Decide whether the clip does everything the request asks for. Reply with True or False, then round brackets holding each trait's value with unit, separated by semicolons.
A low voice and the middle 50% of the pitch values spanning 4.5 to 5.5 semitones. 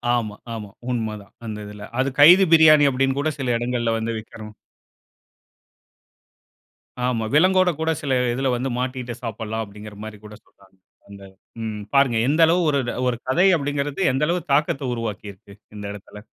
True (120 Hz; 4.8 semitones)